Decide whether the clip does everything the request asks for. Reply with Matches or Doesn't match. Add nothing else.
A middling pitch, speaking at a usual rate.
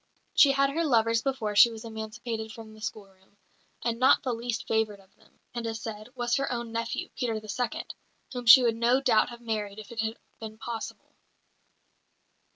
Doesn't match